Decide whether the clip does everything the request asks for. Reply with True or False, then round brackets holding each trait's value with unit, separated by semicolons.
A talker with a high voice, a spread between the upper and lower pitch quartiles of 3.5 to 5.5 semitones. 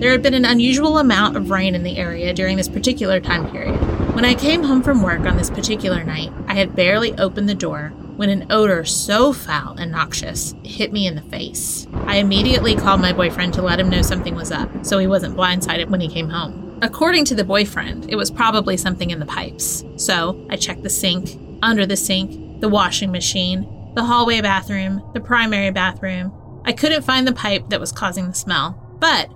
True (195 Hz; 3.9 semitones)